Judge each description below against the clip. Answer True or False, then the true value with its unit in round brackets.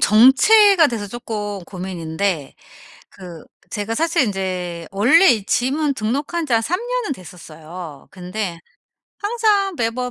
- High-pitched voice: True (220 Hz)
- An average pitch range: False (9.0 semitones)